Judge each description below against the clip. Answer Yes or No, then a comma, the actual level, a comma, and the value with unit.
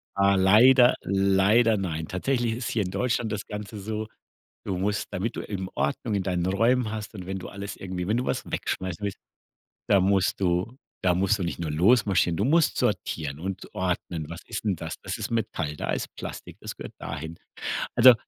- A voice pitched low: Yes, low, 100 Hz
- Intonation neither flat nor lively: Yes, average, 3.3 semitones